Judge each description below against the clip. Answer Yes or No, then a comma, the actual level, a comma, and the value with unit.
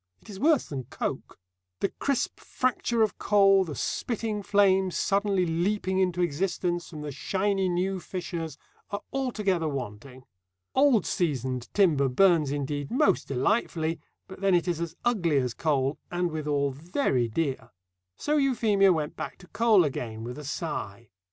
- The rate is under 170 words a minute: Yes, average, 150 wpm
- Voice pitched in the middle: Yes, medium, 175 Hz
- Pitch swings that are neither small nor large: No, wide, 5.7 semitones